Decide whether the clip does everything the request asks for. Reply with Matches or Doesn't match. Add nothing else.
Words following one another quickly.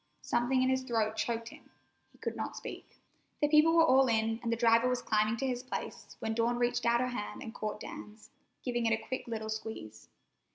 Matches